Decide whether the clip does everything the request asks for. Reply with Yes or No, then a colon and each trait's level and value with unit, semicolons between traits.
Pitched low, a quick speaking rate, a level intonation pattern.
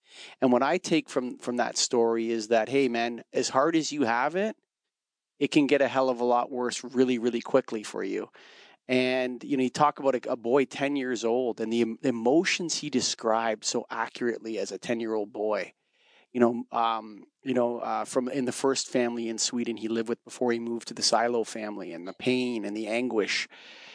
Yes: low, 120 Hz; fast, 215 wpm; narrow, 2.3 semitones